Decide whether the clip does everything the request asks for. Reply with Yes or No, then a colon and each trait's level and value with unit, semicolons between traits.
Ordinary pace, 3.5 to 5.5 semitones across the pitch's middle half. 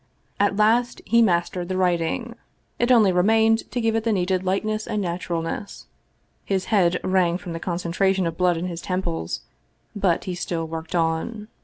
Yes: average, 170 wpm; average, 3.8 semitones